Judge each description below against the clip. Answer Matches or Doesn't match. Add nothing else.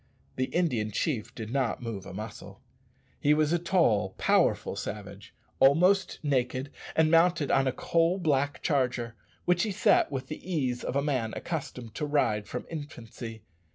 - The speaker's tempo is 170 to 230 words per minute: Doesn't match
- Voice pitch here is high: Doesn't match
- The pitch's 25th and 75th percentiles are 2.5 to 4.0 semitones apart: Doesn't match